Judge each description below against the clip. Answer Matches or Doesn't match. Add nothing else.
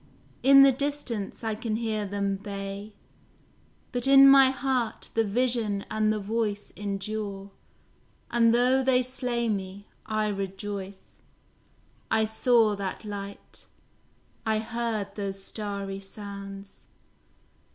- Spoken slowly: Matches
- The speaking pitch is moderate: Doesn't match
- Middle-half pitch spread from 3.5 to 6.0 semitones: Doesn't match